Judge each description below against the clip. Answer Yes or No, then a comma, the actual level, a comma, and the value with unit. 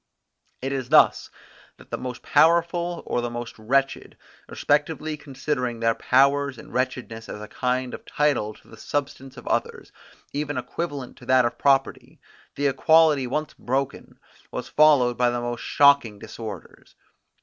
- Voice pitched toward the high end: No, low, 130 Hz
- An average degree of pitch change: Yes, average, 3.2 semitones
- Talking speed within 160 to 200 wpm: No, average, 150 wpm